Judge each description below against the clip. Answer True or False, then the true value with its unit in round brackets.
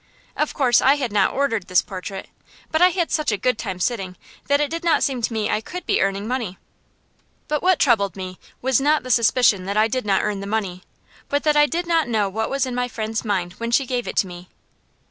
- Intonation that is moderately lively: False (6.0 semitones)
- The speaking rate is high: True (240 wpm)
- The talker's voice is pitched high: True (230 Hz)